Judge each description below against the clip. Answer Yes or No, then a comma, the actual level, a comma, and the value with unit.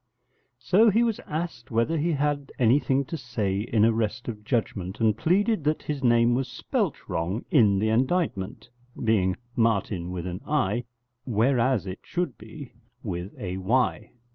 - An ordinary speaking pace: Yes, average, 155 wpm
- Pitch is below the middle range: Yes, low, 120 Hz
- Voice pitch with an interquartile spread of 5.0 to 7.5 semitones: Yes, wide, 5.6 semitones